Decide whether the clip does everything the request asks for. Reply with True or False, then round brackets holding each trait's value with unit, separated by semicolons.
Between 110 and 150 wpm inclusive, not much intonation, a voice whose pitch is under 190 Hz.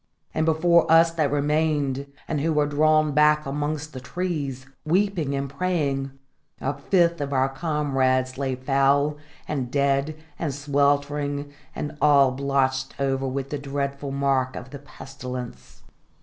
True (140 wpm; 2.0 semitones; 140 Hz)